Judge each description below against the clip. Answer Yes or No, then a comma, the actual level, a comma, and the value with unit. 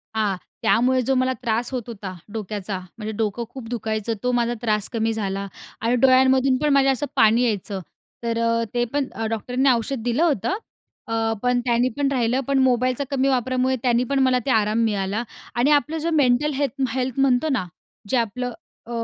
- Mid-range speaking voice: No, high, 245 Hz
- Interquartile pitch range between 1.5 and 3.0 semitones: Yes, average, 2.7 semitones